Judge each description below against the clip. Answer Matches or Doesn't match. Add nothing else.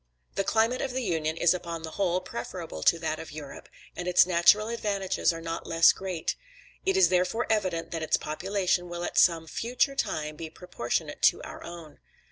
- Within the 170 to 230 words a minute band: Matches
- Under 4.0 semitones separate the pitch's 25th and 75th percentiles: Matches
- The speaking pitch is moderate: Matches